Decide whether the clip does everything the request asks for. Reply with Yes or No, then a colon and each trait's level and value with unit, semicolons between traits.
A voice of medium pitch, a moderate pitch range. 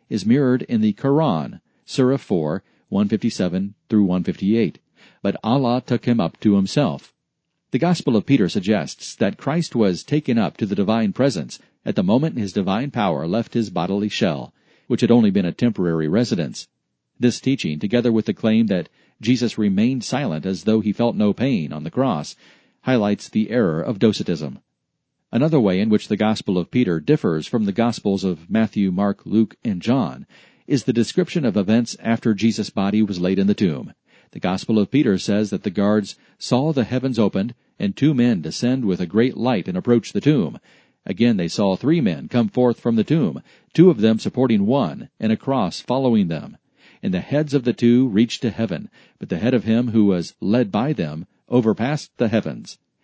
No: low, 115 Hz; average, 3.9 semitones